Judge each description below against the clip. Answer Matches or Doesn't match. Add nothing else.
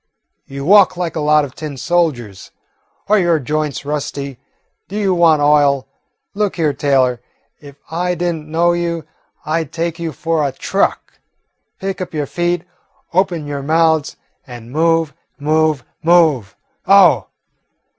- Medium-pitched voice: Matches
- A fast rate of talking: Doesn't match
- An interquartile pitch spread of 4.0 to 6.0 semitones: Doesn't match